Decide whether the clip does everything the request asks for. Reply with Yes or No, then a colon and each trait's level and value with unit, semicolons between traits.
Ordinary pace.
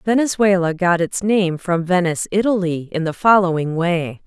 Yes: average, 155 wpm